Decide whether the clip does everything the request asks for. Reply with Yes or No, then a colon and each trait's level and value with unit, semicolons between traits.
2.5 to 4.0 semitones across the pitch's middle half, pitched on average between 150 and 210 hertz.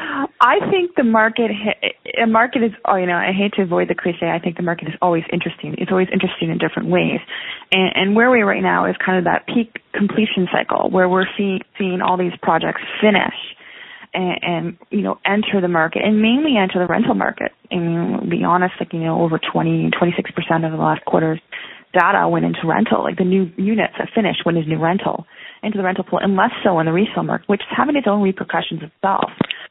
Yes: average, 3.6 semitones; high, 190 Hz